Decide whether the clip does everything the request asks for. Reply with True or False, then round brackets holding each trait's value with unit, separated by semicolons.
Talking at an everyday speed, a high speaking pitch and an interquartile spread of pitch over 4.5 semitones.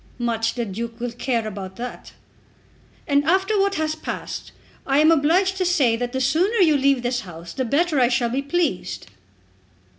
True (180 wpm; 265 Hz; 5.4 semitones)